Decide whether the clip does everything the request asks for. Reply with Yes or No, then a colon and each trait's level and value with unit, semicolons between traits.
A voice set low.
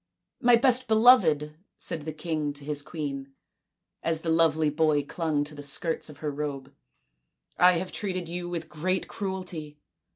No: medium, 160 Hz